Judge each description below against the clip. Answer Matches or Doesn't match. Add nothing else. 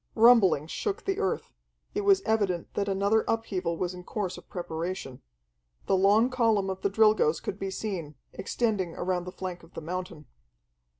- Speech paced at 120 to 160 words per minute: Doesn't match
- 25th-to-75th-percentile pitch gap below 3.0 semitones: Doesn't match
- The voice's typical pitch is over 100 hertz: Matches